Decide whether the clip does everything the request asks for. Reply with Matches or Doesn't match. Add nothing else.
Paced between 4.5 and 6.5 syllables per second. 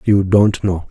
Doesn't match